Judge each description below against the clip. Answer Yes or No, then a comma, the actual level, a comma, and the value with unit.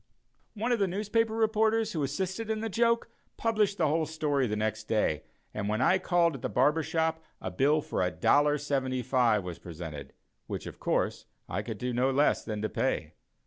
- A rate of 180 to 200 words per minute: Yes, average, 185 wpm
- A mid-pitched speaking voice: Yes, medium, 150 Hz